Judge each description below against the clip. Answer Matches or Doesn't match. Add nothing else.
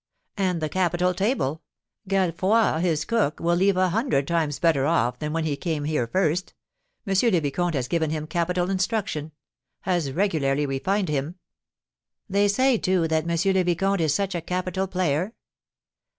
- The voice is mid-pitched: Matches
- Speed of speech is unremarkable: Matches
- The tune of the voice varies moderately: Matches